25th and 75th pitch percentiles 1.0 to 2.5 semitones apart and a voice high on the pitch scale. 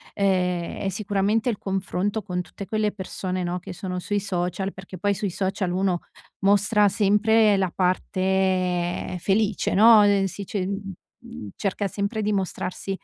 Yes: narrow, 2.0 semitones; high, 195 Hz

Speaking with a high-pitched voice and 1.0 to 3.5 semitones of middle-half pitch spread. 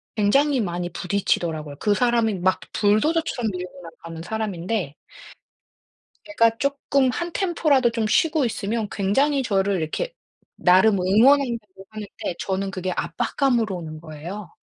No: high, 210 Hz; wide, 5.5 semitones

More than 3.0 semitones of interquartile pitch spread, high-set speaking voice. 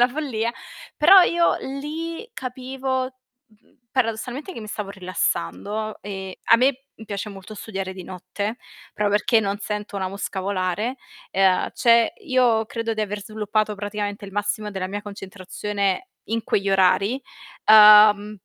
Yes: average, 3.4 semitones; high, 210 Hz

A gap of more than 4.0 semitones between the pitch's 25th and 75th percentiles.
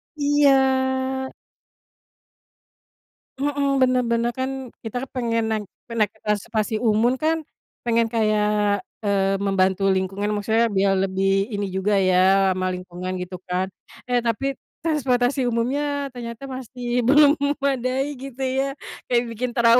Yes: average, 4.7 semitones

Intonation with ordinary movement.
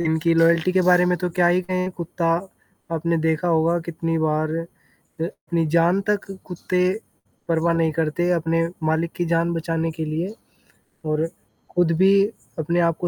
No: narrow, 1.6 semitones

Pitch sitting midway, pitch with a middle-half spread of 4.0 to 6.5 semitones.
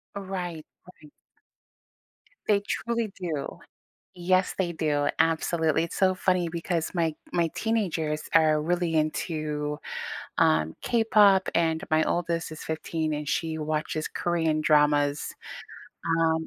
No: medium, 165 Hz; narrow, 2.5 semitones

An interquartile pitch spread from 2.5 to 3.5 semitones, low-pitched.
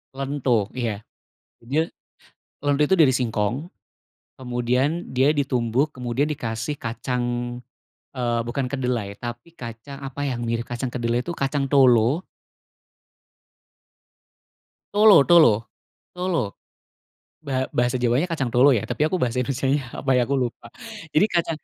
Yes: average, 3.2 semitones; low, 130 Hz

